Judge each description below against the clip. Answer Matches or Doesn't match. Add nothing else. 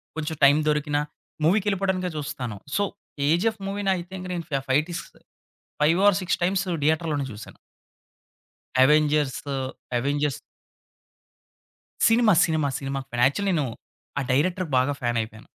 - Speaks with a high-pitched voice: Doesn't match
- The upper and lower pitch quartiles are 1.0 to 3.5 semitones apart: Doesn't match